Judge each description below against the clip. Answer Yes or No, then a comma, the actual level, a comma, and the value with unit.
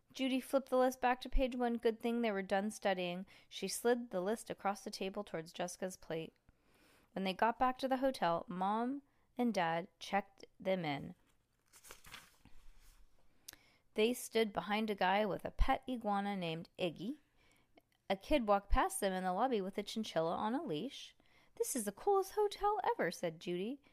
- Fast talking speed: No, average, 175 wpm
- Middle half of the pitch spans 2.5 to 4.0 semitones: No, average, 5.2 semitones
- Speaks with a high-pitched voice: Yes, high, 210 Hz